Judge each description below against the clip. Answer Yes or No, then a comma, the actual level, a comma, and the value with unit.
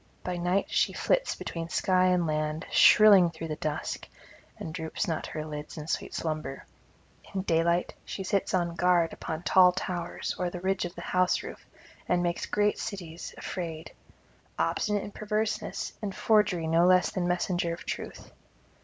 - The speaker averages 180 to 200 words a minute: No, average, 165 wpm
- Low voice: No, medium, 175 Hz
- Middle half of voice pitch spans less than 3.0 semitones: Yes, narrow, 2.4 semitones